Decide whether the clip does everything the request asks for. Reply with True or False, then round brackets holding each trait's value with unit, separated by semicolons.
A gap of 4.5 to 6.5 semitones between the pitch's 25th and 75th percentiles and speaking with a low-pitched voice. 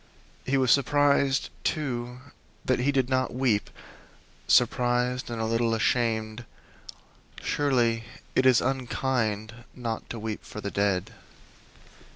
False (2.7 semitones; 120 Hz)